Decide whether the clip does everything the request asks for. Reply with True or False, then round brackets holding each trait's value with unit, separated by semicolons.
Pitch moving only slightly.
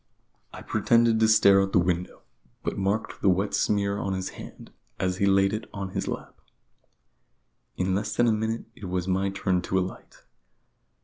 True (2.2 semitones)